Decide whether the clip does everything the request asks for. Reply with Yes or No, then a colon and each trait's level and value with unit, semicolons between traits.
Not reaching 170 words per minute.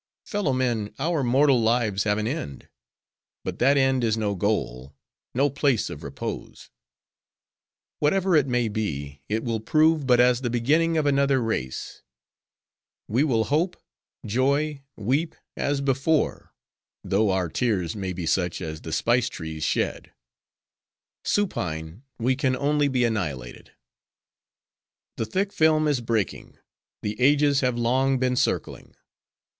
Yes: slow, 135 wpm